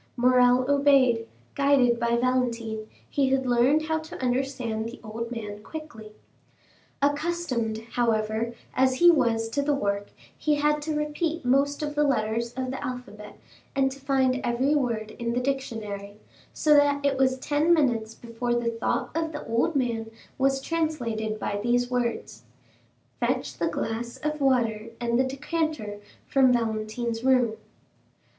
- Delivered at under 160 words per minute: Yes, average, 150 wpm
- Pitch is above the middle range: Yes, very high, 250 Hz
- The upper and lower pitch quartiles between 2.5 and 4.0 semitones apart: Yes, average, 3.6 semitones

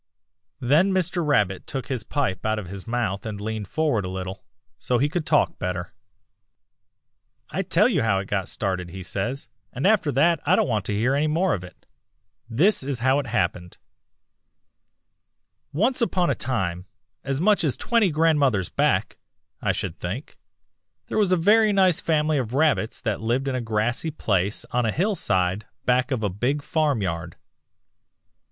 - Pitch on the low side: Yes, low, 125 Hz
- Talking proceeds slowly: No, average, 170 wpm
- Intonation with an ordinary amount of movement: No, wide, 7.4 semitones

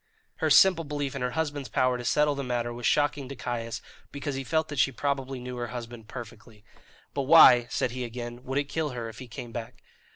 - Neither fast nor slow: No, fast, 225 wpm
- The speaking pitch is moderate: No, low, 125 Hz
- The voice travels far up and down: No, average, 3.0 semitones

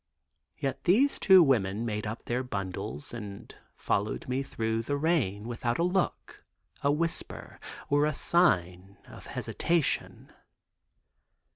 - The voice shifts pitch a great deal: Yes, wide, 7.4 semitones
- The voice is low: Yes, low, 120 Hz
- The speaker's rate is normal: No, slow, 125 wpm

